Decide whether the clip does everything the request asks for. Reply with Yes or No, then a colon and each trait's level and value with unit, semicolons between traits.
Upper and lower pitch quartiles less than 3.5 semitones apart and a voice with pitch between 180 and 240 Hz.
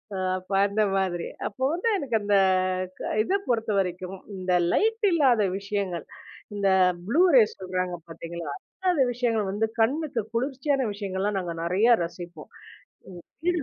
No: wide, 5.5 semitones; high, 205 Hz